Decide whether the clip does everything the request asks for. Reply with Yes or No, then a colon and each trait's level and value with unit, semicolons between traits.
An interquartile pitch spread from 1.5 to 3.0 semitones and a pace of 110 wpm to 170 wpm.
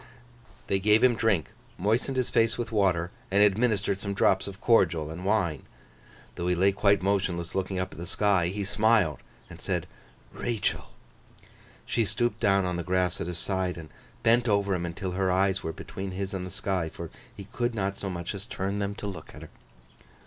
No: narrow, 2.4 semitones; average, 200 wpm